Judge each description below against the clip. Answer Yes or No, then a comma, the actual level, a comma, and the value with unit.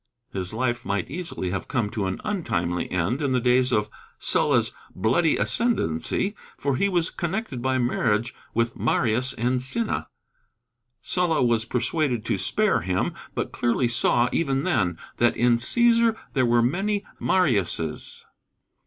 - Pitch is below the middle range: Yes, low, 125 Hz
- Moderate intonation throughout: No, wide, 7.1 semitones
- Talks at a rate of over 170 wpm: No, average, 145 wpm